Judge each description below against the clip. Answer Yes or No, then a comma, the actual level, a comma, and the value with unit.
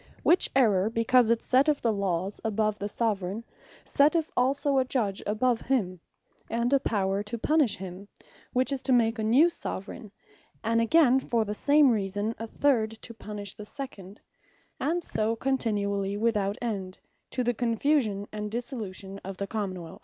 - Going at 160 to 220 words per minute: Yes, average, 165 wpm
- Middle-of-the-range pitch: No, high, 225 Hz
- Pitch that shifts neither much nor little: Yes, average, 4.1 semitones